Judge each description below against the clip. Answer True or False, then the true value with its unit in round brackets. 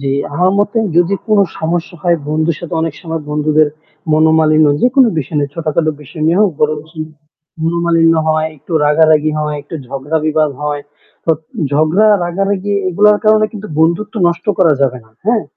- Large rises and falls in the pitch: False (2.9 semitones)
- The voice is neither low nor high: True (160 Hz)